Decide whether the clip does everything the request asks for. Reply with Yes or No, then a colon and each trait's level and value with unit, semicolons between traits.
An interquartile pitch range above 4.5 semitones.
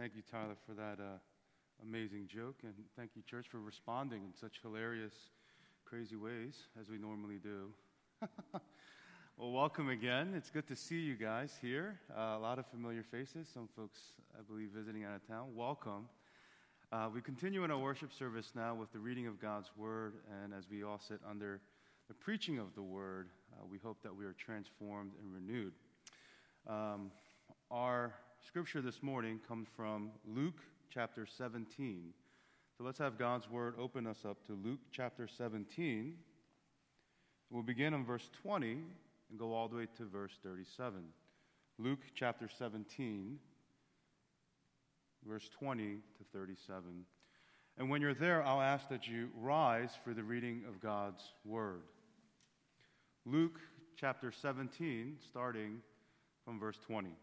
No: average, 3.4 semitones